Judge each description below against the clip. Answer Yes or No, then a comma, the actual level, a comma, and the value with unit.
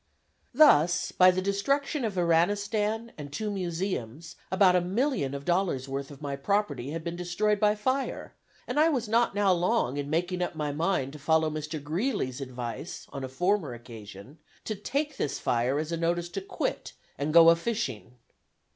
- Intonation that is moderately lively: No, wide, 6.3 semitones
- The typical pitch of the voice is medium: Yes, medium, 175 Hz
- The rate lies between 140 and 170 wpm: No, average, 180 wpm